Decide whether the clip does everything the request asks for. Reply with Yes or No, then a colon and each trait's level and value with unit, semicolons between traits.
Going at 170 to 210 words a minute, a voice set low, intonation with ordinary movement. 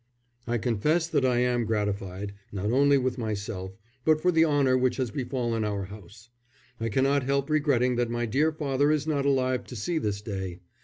Yes: average, 190 wpm; low, 125 Hz; average, 4.9 semitones